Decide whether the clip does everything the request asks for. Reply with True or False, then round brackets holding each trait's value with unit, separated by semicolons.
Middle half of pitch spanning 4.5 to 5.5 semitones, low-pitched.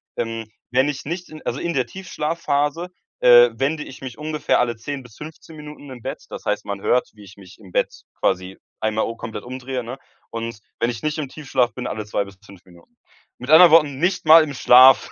True (5.0 semitones; 130 Hz)